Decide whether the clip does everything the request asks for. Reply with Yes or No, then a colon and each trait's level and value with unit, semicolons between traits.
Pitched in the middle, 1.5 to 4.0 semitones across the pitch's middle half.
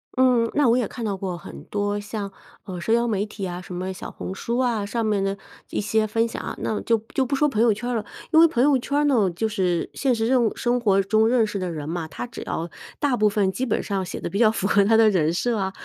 No: high, 215 Hz; average, 3.6 semitones